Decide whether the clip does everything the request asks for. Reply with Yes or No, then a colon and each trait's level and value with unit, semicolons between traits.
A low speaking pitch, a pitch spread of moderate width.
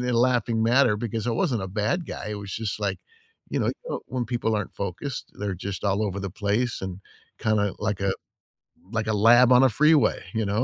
Yes: low, 110 Hz; average, 3.2 semitones